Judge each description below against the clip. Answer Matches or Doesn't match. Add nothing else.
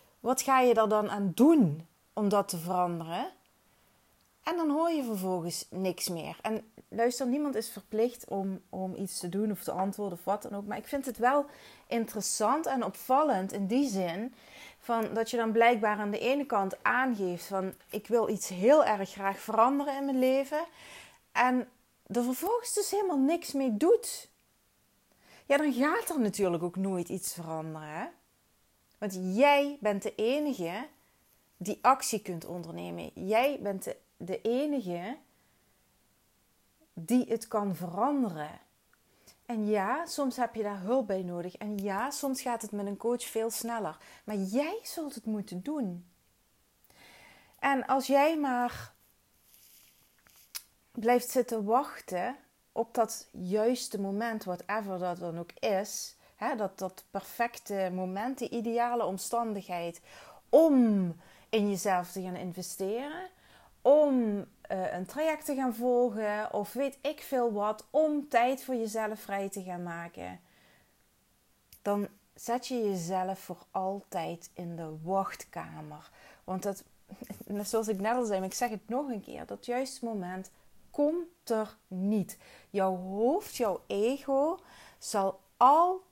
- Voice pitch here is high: Matches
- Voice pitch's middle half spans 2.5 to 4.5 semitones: Doesn't match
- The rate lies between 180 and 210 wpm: Doesn't match